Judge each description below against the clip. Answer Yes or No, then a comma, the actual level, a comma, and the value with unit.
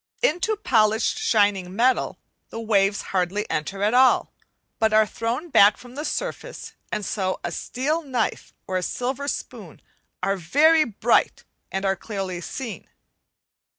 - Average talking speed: Yes, average, 145 wpm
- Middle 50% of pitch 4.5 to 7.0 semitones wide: Yes, average, 5.0 semitones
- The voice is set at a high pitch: Yes, high, 220 Hz